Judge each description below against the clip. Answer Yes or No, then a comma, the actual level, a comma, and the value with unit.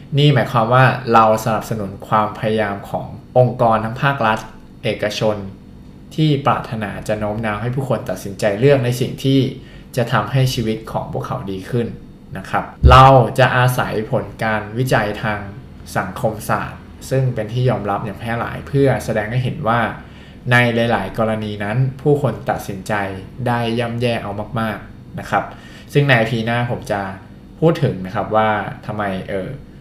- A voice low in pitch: Yes, low, 115 Hz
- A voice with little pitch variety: No, average, 3.3 semitones